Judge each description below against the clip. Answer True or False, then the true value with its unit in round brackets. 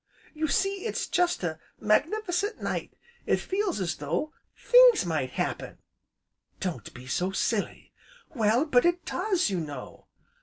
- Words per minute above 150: False (140 wpm)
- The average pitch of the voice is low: False (275 Hz)